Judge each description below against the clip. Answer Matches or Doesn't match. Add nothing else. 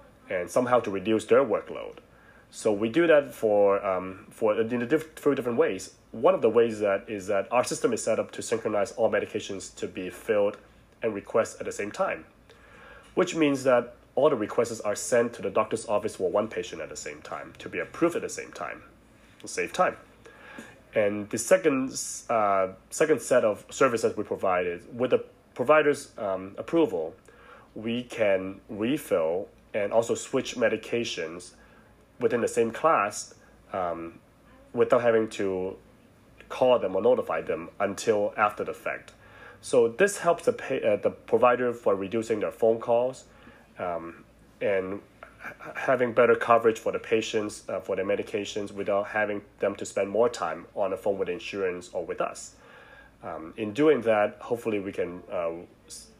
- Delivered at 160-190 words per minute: Matches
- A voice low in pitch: Matches